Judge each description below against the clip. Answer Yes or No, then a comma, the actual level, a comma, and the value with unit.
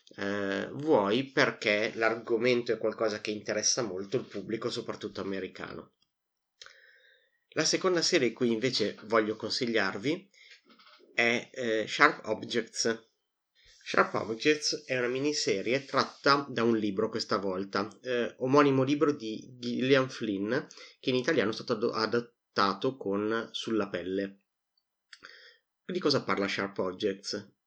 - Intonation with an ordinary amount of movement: Yes, average, 3.4 semitones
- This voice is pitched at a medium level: No, low, 115 Hz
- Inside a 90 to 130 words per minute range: Yes, average, 120 wpm